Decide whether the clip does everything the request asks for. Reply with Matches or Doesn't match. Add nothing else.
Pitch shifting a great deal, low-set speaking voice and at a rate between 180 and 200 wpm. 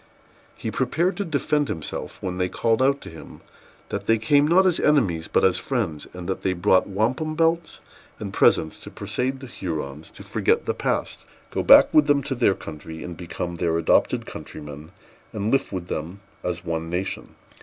Matches